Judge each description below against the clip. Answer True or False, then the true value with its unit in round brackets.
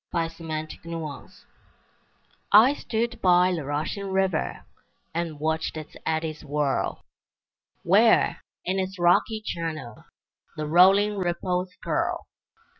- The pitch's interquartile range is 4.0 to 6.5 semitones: False (3.4 semitones)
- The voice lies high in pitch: False (170 Hz)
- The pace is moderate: False (115 wpm)